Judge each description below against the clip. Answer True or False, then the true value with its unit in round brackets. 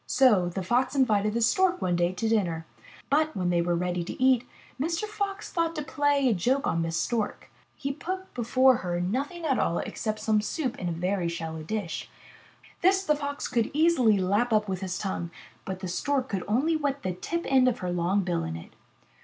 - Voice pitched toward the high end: True (225 Hz)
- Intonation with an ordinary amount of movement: False (7.8 semitones)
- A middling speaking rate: False (210 wpm)